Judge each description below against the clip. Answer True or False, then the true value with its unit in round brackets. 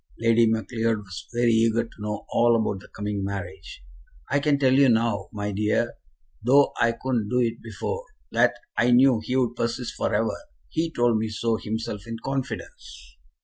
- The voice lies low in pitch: True (115 Hz)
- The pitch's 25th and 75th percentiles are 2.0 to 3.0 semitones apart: True (2.5 semitones)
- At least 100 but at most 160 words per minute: False (175 wpm)